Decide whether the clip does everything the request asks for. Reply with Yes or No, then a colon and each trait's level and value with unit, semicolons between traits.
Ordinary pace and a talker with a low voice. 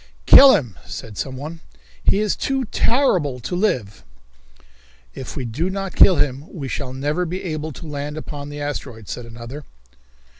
No: average, 160 wpm; medium, 145 Hz